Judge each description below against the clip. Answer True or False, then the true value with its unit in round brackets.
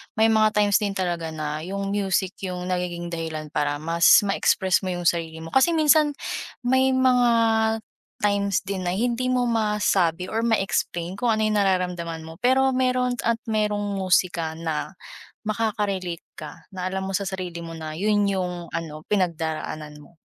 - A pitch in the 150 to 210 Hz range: True (190 Hz)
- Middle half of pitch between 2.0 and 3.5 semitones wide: False (4.2 semitones)